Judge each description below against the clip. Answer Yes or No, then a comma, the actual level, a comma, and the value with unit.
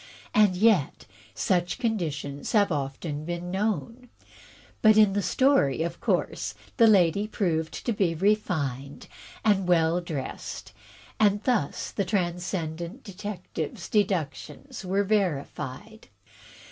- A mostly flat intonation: No, average, 4.7 semitones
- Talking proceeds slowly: Yes, slow, 110 wpm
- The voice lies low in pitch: No, medium, 185 Hz